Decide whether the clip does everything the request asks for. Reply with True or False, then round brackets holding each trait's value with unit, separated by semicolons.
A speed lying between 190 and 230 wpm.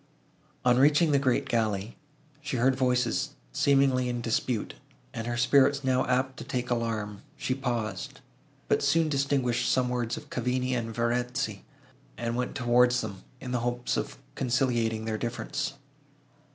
False (150 wpm)